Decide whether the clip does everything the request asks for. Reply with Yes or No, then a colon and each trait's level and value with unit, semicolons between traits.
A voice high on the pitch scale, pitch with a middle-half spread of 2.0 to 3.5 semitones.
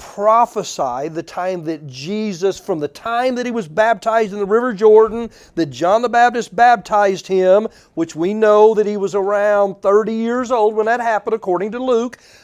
Yes: high, 215 Hz; average, 3.2 semitones